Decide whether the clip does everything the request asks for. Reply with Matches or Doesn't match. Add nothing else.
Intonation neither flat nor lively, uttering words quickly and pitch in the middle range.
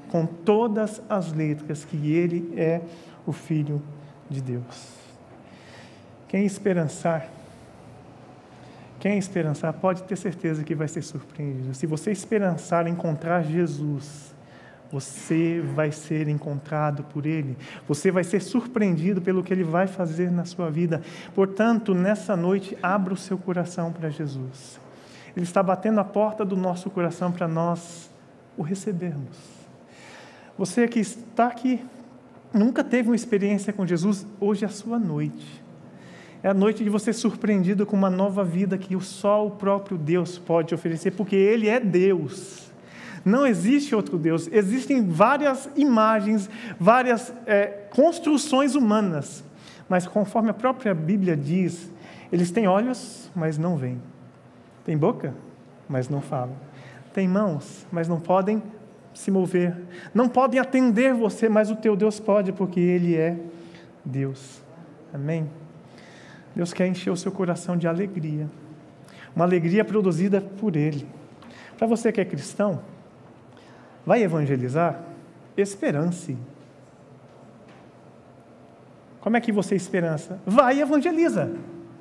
Doesn't match